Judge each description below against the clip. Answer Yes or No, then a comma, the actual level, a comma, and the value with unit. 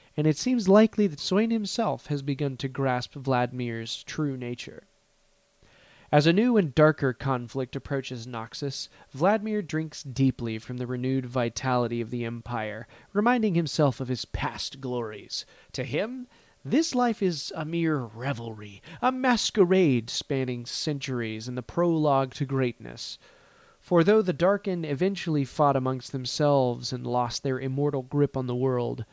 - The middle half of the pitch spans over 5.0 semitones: Yes, wide, 5.4 semitones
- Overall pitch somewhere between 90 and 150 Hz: Yes, low, 135 Hz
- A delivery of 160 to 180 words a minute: No, average, 145 wpm